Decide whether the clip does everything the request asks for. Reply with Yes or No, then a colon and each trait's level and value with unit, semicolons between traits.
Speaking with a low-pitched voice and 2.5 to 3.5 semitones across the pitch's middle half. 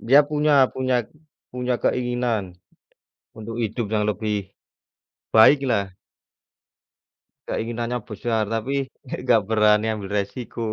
Yes: low, 115 Hz; average, 2.8 semitones